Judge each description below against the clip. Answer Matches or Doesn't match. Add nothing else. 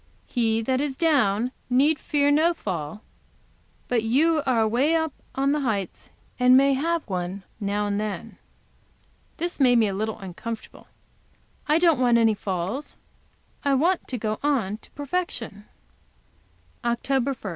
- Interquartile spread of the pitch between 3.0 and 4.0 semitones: Doesn't match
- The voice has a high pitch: Matches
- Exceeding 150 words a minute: Doesn't match